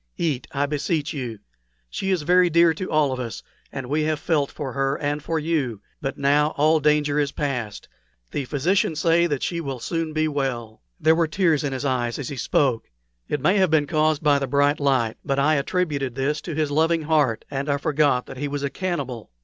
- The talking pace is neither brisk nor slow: No, fast, 220 wpm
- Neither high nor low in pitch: Yes, medium, 145 Hz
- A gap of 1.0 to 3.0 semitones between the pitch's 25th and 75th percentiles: Yes, narrow, 2.6 semitones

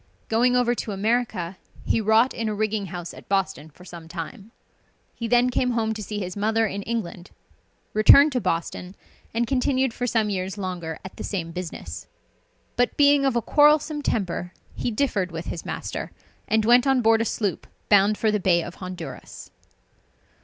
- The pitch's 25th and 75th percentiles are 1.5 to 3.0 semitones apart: No, average, 4.7 semitones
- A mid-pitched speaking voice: No, high, 215 Hz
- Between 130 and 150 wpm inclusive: No, average, 180 wpm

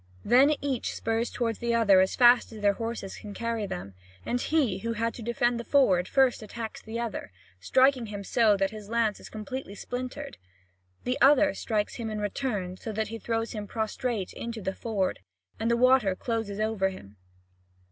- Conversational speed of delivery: Yes, average, 190 wpm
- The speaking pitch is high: Yes, high, 225 Hz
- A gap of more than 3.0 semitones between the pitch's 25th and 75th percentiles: No, average, 2.7 semitones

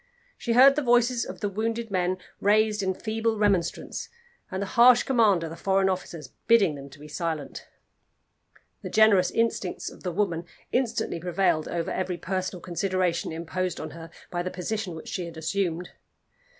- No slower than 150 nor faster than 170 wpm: Yes, average, 165 wpm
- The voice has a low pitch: No, medium, 185 Hz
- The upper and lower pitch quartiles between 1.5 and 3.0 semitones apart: No, average, 4.2 semitones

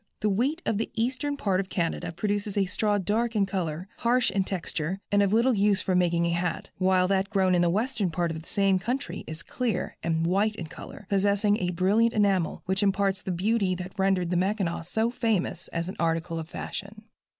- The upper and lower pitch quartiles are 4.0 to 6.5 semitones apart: No, average, 3.0 semitones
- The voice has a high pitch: Yes, high, 195 Hz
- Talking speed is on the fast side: Yes, fast, 210 wpm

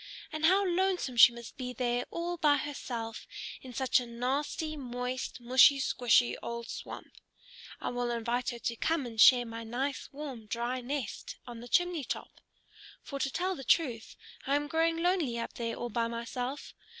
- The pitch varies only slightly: No, average, 3.7 semitones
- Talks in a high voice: Yes, very high, 250 Hz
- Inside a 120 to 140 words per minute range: No, average, 175 wpm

